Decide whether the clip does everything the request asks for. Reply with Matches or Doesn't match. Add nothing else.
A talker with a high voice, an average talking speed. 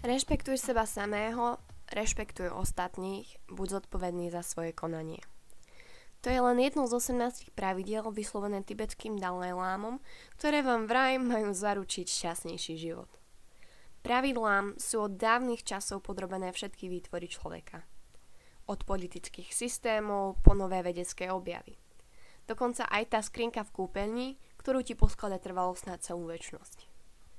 Matches